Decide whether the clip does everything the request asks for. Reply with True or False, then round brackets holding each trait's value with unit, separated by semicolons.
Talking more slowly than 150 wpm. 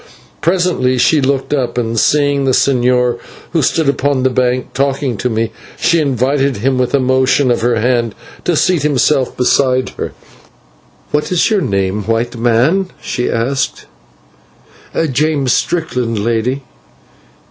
True (140 wpm)